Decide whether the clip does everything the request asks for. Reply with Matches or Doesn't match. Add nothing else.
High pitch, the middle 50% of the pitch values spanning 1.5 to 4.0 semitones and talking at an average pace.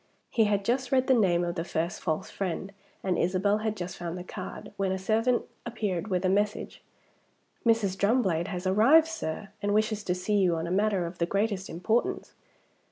Matches